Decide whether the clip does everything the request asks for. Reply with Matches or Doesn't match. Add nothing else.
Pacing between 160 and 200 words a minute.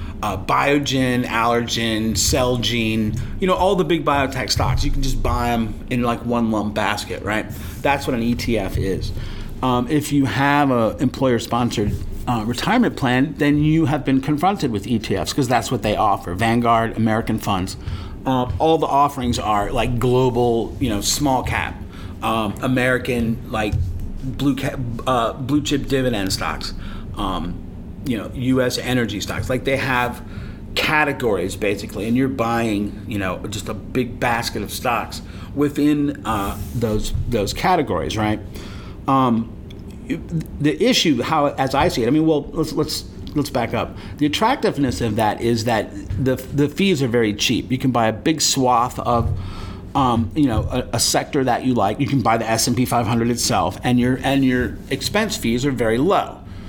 Matches